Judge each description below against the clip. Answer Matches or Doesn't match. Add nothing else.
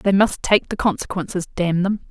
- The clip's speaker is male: Doesn't match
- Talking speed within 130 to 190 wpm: Doesn't match